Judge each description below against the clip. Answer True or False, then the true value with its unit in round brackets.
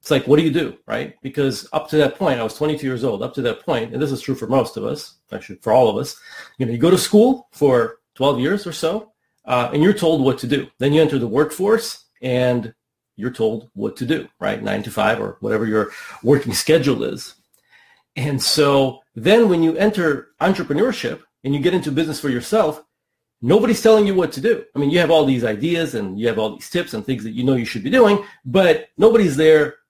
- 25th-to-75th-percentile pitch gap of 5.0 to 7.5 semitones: True (5.4 semitones)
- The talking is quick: True (235 wpm)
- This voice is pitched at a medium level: True (150 Hz)